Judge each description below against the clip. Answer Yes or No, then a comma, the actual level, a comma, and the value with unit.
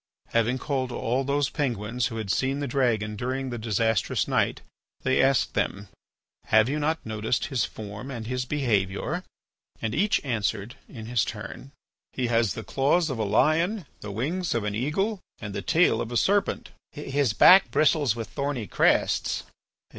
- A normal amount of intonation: Yes, average, 4.5 semitones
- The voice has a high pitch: No, low, 125 Hz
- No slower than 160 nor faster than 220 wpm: Yes, average, 170 wpm